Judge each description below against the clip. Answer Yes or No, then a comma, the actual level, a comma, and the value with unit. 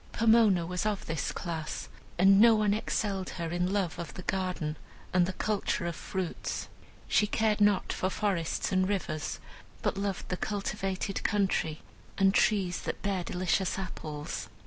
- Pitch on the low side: No, high, 190 Hz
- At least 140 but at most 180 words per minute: Yes, average, 155 wpm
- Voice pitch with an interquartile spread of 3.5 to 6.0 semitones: No, narrow, 2.6 semitones